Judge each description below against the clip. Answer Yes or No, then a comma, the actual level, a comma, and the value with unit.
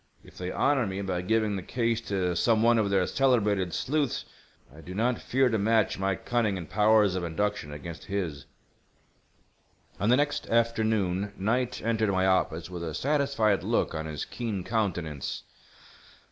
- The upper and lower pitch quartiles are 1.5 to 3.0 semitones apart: No, average, 4.1 semitones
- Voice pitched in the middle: No, low, 105 Hz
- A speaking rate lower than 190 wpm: Yes, average, 165 wpm